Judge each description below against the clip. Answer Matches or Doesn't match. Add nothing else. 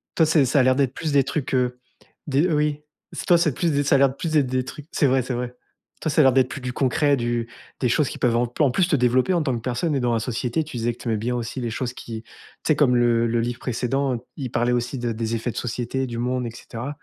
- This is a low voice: Matches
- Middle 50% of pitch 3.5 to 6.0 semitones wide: Doesn't match